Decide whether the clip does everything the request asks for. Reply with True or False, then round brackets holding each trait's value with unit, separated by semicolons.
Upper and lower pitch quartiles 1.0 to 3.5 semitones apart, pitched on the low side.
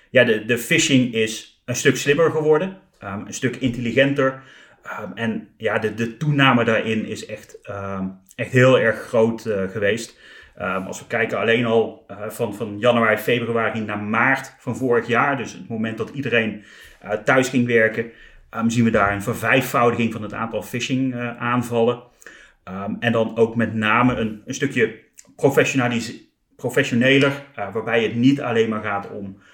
True (2.7 semitones; 115 Hz)